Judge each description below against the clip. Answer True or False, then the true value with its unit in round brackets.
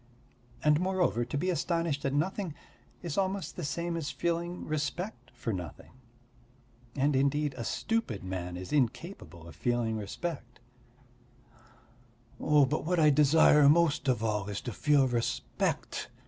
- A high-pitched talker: False (145 Hz)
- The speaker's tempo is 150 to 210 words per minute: False (135 wpm)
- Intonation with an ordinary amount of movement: False (5.9 semitones)